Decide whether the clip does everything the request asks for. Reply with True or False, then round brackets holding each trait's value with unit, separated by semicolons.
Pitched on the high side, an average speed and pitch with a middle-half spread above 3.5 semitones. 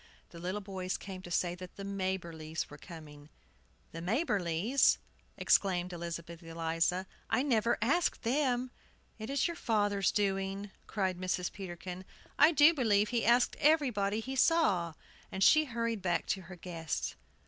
True (195 Hz; 150 wpm; 5.1 semitones)